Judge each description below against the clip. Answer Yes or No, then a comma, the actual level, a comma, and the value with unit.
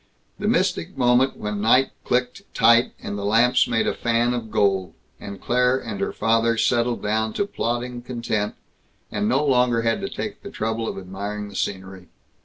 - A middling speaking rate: Yes, average, 180 wpm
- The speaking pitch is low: Yes, low, 115 Hz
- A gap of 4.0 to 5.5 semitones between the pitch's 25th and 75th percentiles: No, average, 3.0 semitones